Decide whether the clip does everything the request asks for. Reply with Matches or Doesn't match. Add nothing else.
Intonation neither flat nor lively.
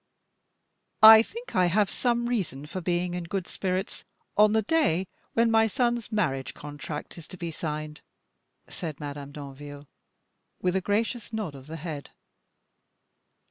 Doesn't match